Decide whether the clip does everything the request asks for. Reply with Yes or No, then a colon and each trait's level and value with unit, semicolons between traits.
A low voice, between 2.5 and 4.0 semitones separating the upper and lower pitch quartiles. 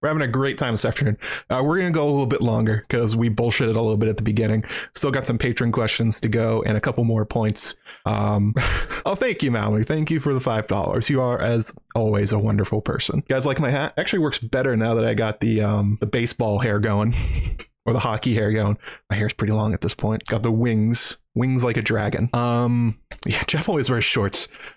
Yes: low, 115 Hz; average, 2.9 semitones